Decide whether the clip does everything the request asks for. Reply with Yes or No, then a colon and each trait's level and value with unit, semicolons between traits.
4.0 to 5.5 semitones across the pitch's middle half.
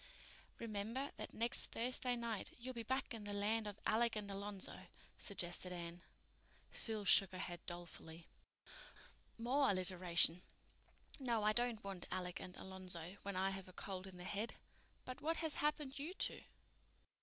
Yes: average, 4.3 semitones